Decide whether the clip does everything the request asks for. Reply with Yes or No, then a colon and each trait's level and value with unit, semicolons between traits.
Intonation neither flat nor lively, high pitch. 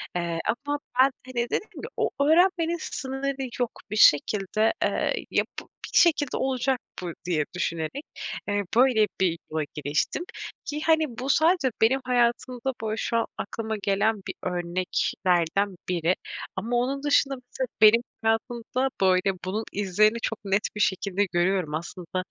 No: wide, 6.1 semitones; high, 220 Hz